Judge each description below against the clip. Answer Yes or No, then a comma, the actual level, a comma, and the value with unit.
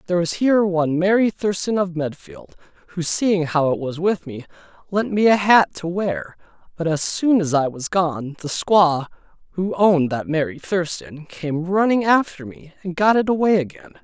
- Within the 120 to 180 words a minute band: No, average, 190 wpm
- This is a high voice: No, medium, 175 Hz